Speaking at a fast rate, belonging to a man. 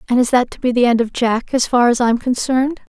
No: fast, 285 wpm; female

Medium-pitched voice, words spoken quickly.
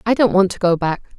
No: high, 195 Hz; fast, 305 wpm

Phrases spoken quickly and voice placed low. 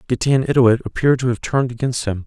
No: average, 185 wpm; low, 125 Hz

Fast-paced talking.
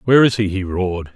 Yes: fast, 260 wpm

